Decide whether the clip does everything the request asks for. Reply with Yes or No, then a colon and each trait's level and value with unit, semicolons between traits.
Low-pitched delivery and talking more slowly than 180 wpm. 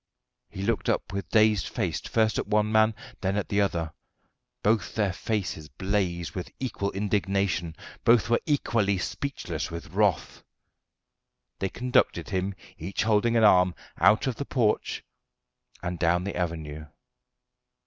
Yes: low, 100 Hz; average, 140 wpm